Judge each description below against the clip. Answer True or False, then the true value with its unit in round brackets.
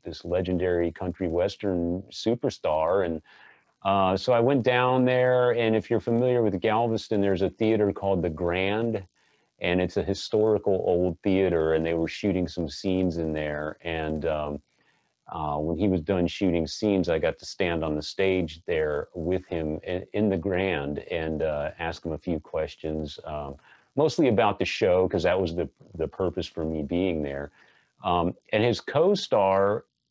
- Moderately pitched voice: False (90 Hz)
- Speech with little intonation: False (3.8 semitones)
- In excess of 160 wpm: True (175 wpm)